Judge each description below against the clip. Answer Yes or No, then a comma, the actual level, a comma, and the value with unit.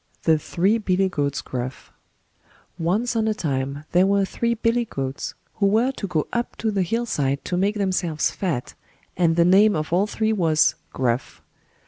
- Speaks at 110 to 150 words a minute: No, average, 175 wpm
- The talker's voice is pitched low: No, medium, 185 Hz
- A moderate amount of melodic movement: No, wide, 5.8 semitones